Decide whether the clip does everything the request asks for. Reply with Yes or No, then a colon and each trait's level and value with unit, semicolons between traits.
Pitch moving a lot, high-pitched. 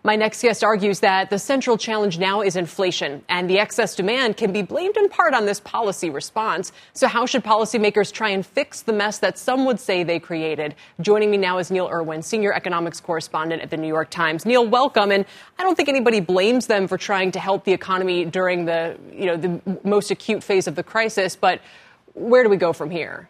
No: average, 3.6 semitones; high, 200 Hz